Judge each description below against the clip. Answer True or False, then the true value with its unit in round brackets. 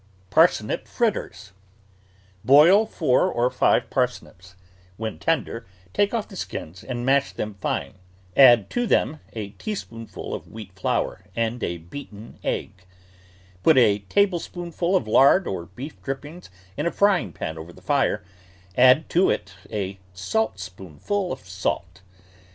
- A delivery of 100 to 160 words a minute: True (140 wpm)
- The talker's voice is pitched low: True (115 Hz)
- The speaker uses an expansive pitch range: True (9.0 semitones)